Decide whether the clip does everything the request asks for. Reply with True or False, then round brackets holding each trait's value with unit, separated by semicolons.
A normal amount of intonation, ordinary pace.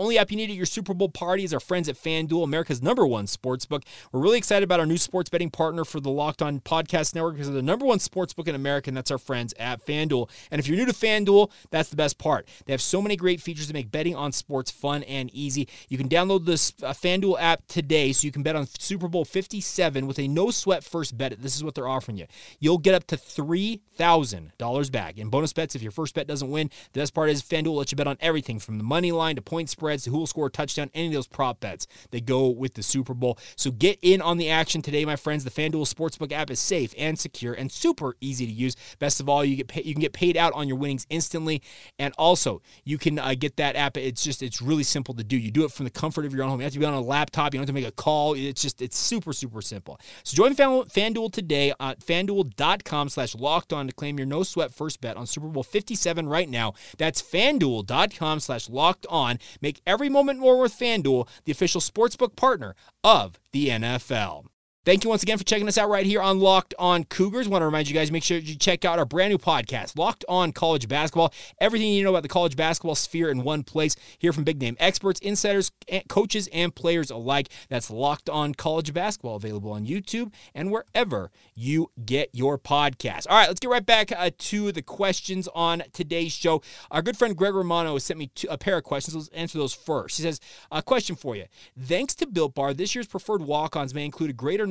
False (4.7 semitones; 245 wpm)